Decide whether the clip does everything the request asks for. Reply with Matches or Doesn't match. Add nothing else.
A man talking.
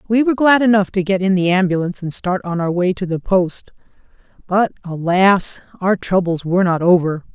Doesn't match